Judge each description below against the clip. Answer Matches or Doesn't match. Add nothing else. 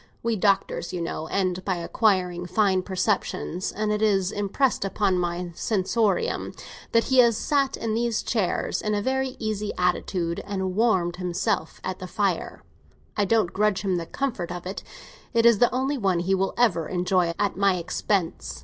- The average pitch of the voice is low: Doesn't match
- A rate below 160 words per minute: Doesn't match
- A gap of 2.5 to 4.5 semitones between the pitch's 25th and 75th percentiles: Matches